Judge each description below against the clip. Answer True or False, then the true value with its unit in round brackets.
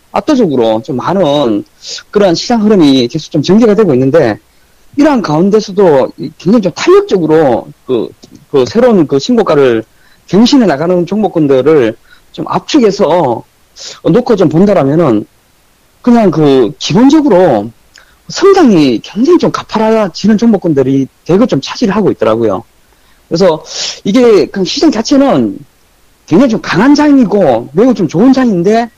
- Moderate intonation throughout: False (7.3 semitones)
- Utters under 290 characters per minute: False (295 characters per minute)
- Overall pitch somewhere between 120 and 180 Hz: False (210 Hz)